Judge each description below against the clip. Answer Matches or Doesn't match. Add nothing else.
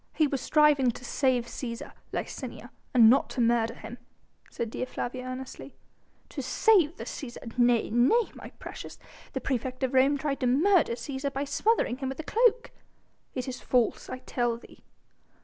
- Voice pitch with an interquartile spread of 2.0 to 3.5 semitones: Matches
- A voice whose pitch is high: Matches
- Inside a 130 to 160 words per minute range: Doesn't match